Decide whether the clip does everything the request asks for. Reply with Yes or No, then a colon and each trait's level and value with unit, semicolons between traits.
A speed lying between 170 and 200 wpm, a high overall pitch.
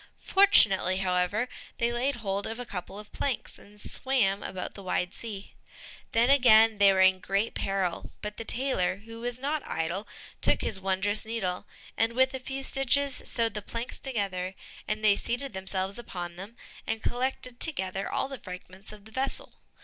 Yes: average, 175 wpm; high, 215 Hz